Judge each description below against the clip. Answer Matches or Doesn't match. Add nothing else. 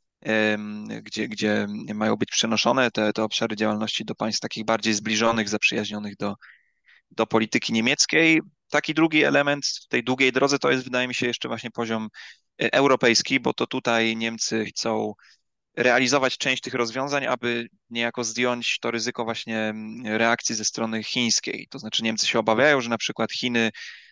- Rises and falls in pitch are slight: Matches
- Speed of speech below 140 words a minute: Doesn't match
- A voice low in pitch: Matches